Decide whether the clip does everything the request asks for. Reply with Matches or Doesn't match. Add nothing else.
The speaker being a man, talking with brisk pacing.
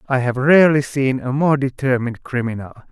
Doesn't match